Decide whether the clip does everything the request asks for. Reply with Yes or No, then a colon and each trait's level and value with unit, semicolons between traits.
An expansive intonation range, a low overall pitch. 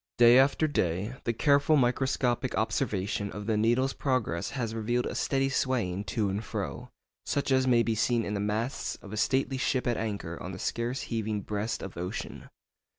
No: average, 3.8 semitones; low, 115 Hz